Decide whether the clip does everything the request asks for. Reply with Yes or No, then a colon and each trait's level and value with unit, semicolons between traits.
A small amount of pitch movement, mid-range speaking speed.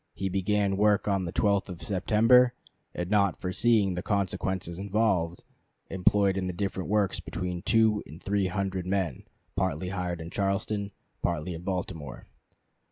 Yes: narrow, 2.2 semitones; average, 150 wpm